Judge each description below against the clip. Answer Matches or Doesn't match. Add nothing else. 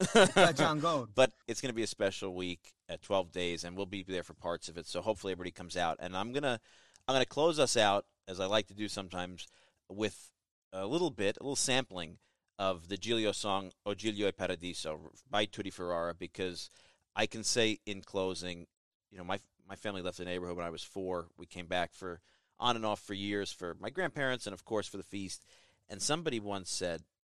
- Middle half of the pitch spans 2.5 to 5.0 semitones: Matches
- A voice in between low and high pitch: Doesn't match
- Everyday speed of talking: Doesn't match